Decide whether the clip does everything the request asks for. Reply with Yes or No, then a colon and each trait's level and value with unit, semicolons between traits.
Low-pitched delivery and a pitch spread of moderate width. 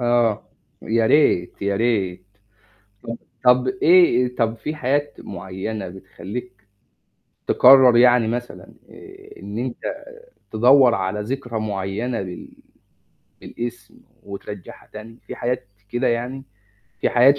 Yes: low, 115 Hz; average, 3.7 semitones